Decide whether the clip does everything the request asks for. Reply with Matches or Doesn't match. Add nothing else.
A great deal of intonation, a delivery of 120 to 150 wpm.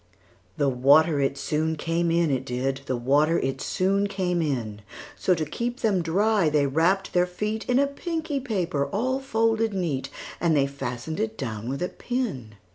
Doesn't match